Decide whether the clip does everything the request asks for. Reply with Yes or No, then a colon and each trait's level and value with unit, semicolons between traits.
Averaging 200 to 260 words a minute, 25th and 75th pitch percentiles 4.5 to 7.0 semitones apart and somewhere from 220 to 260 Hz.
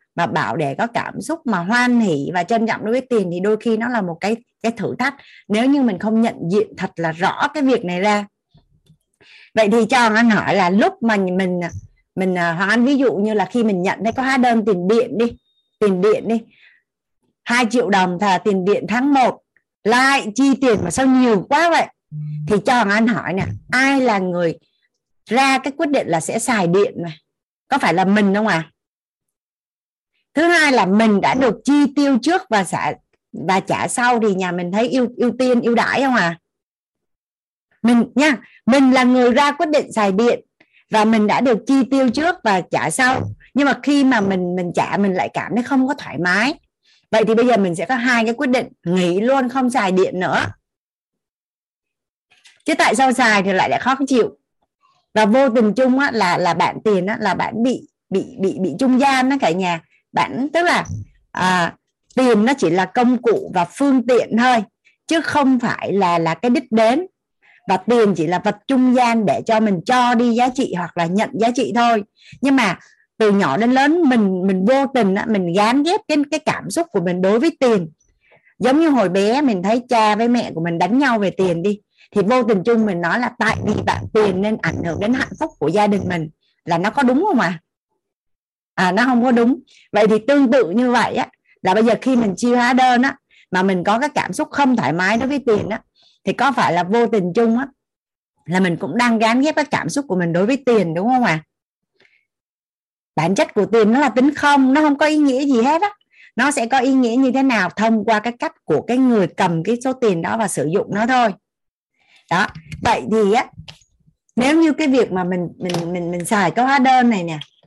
Yes: average, 225 wpm; average, 5.0 semitones; high, 230 Hz